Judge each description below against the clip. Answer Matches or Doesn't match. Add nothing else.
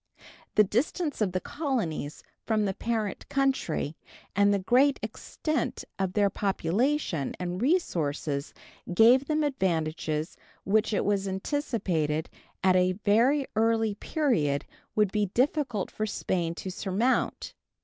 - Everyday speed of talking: Doesn't match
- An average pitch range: Doesn't match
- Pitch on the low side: Doesn't match